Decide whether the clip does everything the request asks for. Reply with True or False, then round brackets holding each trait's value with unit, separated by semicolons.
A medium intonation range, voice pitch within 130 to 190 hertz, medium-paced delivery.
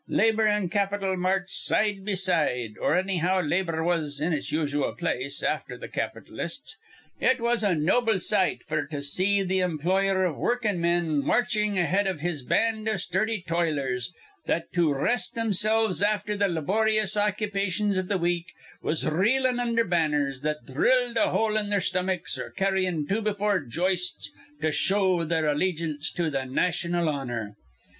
True (4.6 semitones; 185 Hz; 160 wpm)